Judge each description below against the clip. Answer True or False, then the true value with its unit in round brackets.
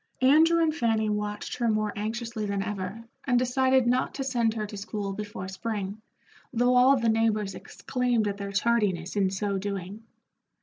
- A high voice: True (215 Hz)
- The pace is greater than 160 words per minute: True (170 wpm)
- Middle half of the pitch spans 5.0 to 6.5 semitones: False (3.4 semitones)